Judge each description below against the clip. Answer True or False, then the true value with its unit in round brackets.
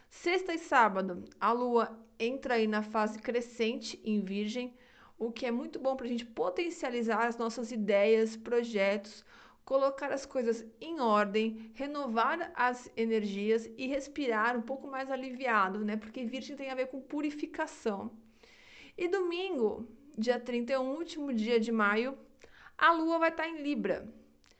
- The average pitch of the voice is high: True (240 Hz)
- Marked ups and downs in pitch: False (3.5 semitones)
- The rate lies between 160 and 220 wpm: False (150 wpm)